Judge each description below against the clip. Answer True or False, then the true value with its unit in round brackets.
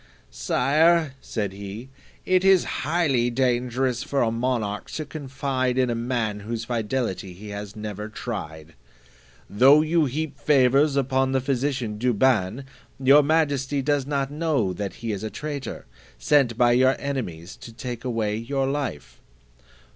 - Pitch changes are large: False (4.3 semitones)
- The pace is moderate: True (145 wpm)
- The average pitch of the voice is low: True (125 Hz)